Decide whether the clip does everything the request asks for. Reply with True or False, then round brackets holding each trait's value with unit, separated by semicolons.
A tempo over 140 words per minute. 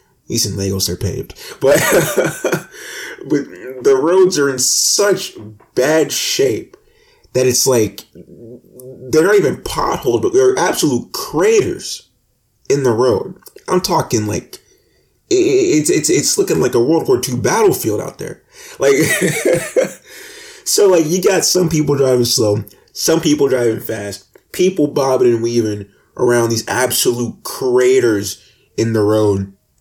False (135 wpm)